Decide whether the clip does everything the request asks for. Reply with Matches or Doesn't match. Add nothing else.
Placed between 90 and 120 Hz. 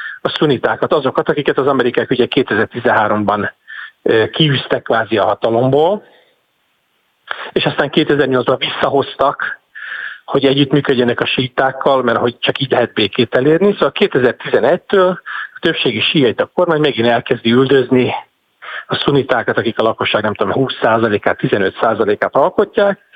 Doesn't match